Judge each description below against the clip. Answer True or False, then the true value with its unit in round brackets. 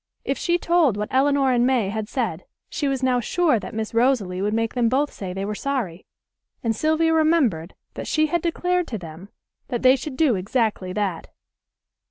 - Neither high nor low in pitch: False (245 Hz)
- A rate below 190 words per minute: False (195 wpm)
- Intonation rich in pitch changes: True (5.8 semitones)